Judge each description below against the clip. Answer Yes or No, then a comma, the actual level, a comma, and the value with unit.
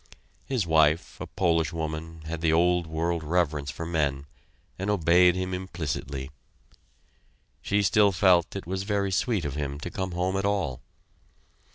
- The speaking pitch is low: Yes, very low, 85 Hz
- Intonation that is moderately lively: Yes, average, 3.0 semitones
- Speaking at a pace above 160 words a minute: No, average, 155 wpm